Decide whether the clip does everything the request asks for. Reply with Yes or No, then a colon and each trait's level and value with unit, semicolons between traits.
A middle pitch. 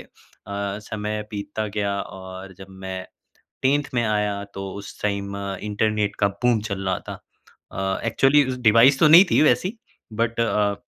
No: low, 105 Hz